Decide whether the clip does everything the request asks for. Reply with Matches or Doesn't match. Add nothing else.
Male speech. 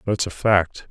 Matches